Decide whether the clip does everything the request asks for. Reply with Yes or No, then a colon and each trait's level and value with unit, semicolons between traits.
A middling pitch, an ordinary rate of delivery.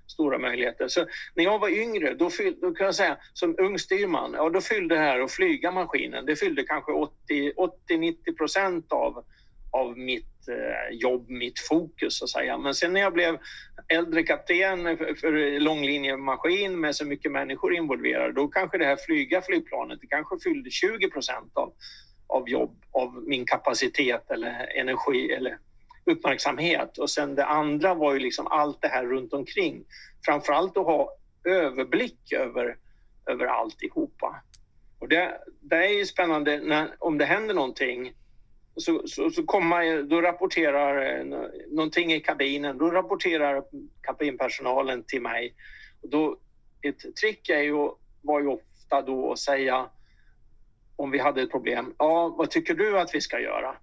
Yes: medium, 165 Hz; average, 160 wpm